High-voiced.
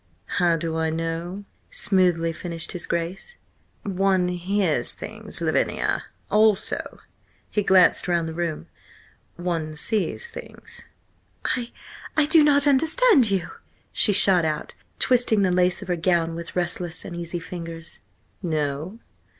No: medium, 180 Hz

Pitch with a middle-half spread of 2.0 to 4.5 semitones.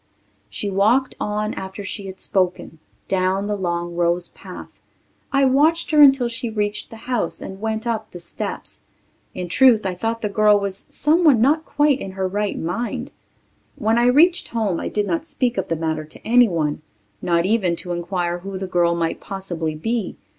No: average, 4.9 semitones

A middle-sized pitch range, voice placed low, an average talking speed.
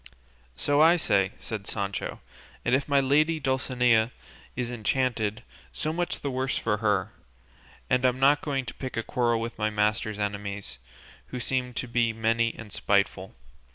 Yes: average, 3.7 semitones; low, 120 Hz; average, 160 wpm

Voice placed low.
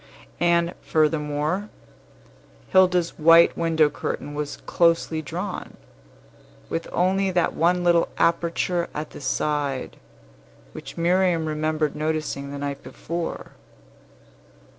No: medium, 165 Hz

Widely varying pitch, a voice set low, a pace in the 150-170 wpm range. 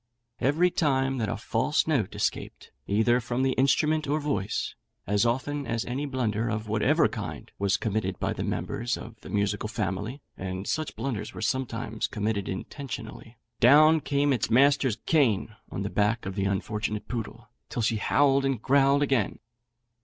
No: average, 4.5 semitones; low, 115 Hz; average, 165 wpm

